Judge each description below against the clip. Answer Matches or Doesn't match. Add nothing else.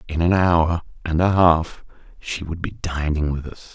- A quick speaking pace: Doesn't match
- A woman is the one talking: Doesn't match